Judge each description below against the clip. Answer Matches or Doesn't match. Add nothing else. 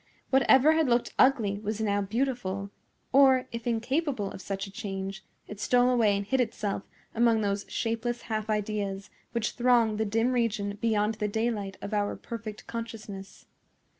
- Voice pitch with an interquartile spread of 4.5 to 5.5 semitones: Doesn't match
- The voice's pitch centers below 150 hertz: Doesn't match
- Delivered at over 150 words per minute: Matches